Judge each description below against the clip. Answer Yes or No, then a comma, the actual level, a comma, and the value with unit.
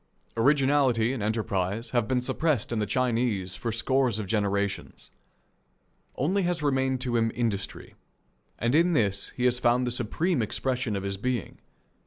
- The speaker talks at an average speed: Yes, average, 155 wpm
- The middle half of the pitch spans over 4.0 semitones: No, average, 3.7 semitones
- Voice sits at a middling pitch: No, low, 120 Hz